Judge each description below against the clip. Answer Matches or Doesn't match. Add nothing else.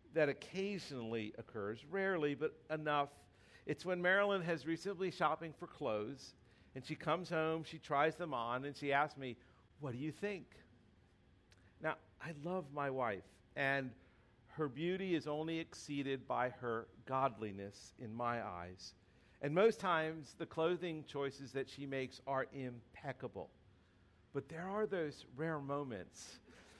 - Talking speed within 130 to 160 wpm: Matches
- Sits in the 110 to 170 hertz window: Matches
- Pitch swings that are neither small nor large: Doesn't match